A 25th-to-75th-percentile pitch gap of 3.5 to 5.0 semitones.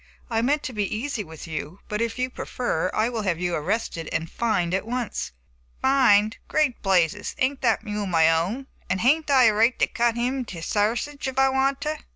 No: wide, 5.5 semitones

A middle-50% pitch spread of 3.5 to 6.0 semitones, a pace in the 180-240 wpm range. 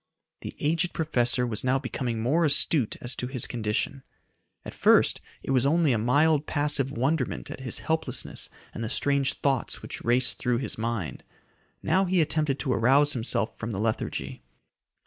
No: average, 3.9 semitones; average, 165 wpm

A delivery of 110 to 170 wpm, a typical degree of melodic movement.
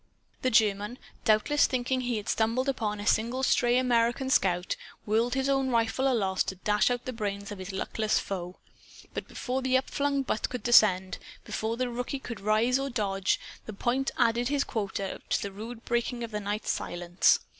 No: average, 185 wpm; average, 3.6 semitones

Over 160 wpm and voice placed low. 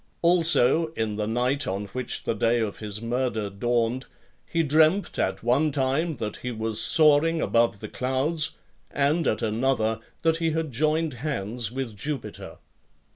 No: average, 155 wpm; low, 130 Hz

